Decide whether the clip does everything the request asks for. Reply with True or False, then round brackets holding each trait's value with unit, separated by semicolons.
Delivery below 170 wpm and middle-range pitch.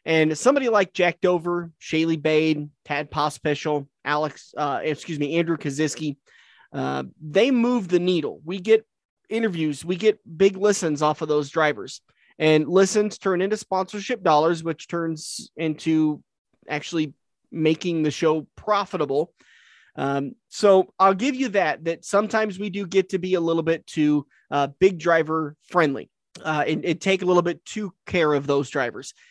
True (160 wpm; 165 Hz)